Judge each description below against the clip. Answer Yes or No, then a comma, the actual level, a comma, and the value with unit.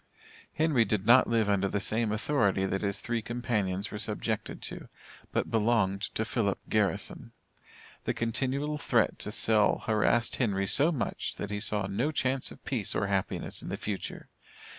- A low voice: Yes, low, 110 Hz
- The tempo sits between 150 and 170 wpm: Yes, average, 165 wpm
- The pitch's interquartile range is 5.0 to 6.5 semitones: No, average, 3.2 semitones